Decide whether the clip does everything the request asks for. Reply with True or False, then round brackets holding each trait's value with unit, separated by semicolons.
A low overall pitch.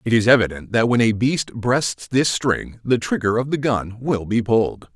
True (115 Hz)